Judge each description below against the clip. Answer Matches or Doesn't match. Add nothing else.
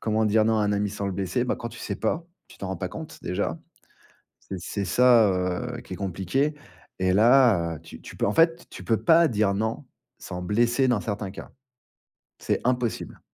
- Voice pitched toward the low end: Matches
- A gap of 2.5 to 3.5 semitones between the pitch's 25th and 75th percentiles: Doesn't match